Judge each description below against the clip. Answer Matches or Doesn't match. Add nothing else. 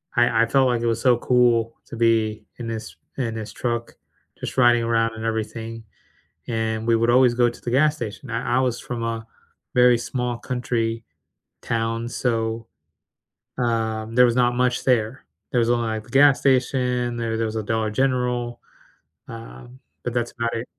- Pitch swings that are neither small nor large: Doesn't match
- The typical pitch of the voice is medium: Doesn't match